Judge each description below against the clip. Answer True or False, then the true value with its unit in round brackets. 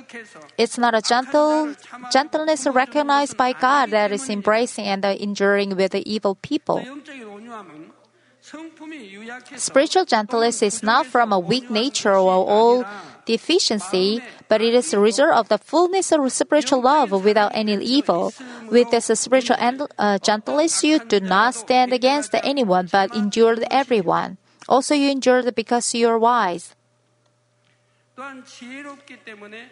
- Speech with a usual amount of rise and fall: True (4.4 semitones)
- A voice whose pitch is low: False (240 Hz)